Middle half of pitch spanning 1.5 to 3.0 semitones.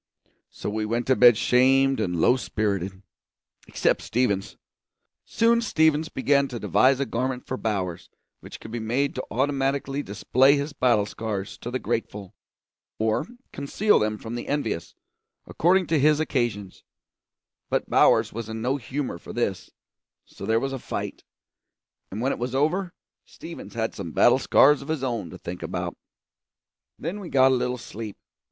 No: average, 4.3 semitones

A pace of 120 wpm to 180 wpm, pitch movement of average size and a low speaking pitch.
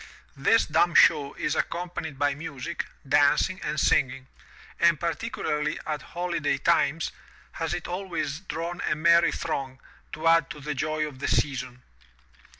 No: average, 145 wpm; average, 3.1 semitones; medium, 155 Hz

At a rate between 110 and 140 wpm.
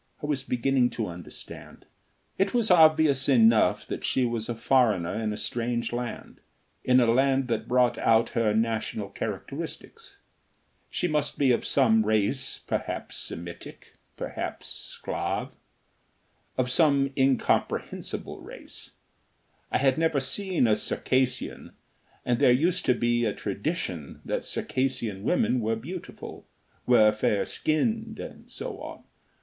Yes: slow, 135 wpm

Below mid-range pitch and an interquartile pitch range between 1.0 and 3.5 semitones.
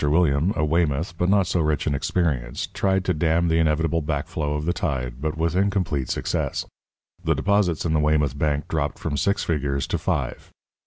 Yes: very low, 80 Hz; average, 2.9 semitones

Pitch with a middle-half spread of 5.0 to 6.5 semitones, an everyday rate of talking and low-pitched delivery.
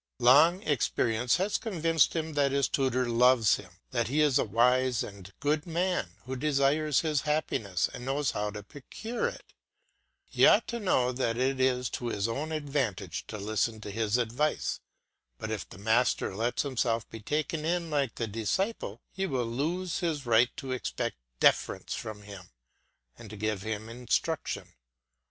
Yes: average, 5.3 semitones; average, 170 wpm; low, 125 Hz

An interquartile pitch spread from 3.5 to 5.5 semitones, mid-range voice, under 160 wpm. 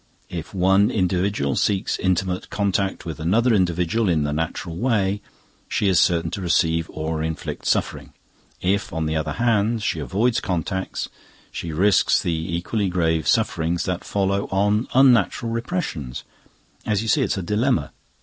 No: average, 4.1 semitones; very low, 95 Hz; average, 150 wpm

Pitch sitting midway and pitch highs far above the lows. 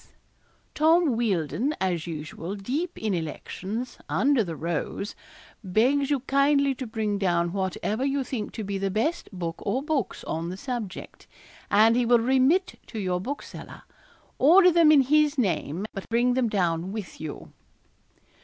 No: high, 225 Hz; wide, 6.7 semitones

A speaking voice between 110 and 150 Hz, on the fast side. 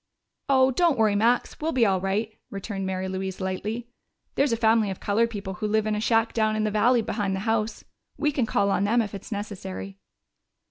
No: high, 215 Hz; fast, 220 wpm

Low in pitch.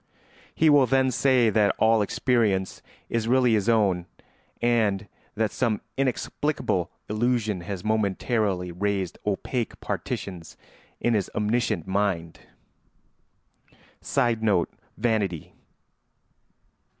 Yes: low, 110 Hz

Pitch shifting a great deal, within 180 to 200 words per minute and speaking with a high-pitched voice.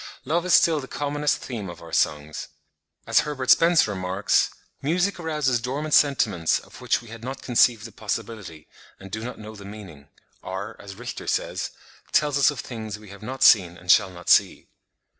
No: wide, 6.4 semitones; average, 185 wpm; low, 115 Hz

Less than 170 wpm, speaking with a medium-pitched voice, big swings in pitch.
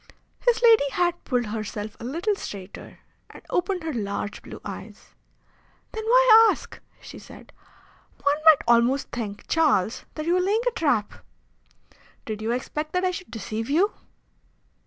No: average, 155 wpm; very high, 300 Hz; wide, 8.6 semitones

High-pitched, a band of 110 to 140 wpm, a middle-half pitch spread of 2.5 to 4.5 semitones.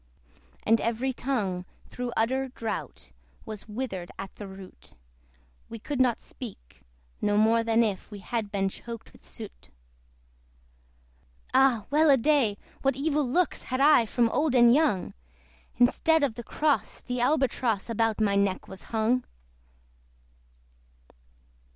Yes: high, 235 Hz; slow, 135 wpm; average, 4.1 semitones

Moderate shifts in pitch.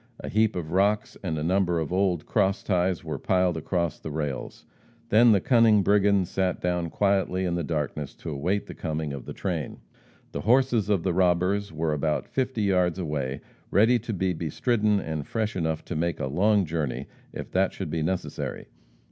Yes: average, 4.0 semitones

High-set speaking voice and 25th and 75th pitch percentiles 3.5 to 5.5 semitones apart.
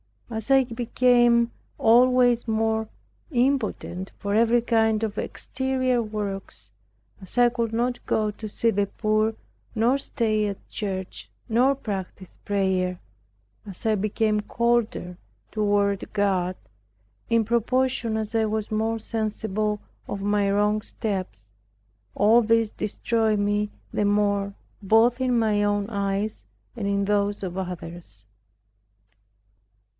No: high, 215 Hz; narrow, 2.5 semitones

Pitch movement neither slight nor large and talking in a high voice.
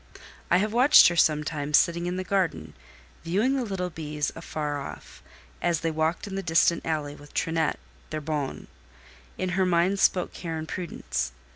No: average, 3.4 semitones; medium, 165 Hz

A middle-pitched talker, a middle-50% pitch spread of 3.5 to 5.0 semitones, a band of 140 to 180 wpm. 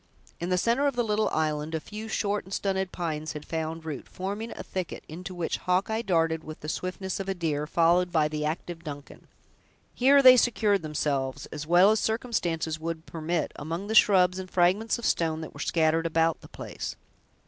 No: medium, 175 Hz; average, 4.0 semitones; average, 195 wpm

